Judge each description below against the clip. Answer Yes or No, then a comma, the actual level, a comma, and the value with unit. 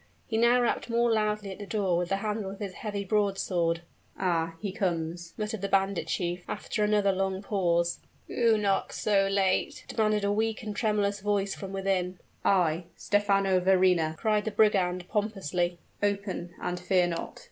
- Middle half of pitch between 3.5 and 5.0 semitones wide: No, average, 2.7 semitones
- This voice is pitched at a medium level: No, high, 195 Hz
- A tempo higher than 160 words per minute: Yes, average, 170 wpm